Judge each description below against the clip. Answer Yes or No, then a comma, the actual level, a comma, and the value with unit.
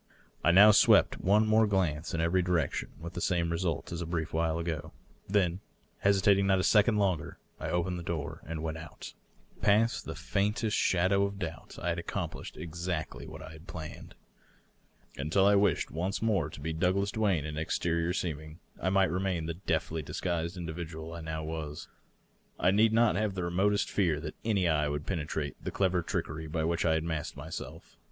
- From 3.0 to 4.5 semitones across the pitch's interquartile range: Yes, average, 3.4 semitones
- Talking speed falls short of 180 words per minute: No, average, 195 wpm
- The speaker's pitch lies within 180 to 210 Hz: No, very low, 85 Hz